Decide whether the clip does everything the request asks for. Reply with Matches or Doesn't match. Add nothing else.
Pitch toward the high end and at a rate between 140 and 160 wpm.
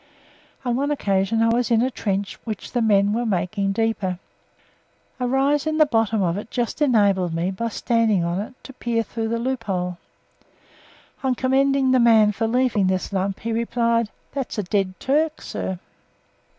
Doesn't match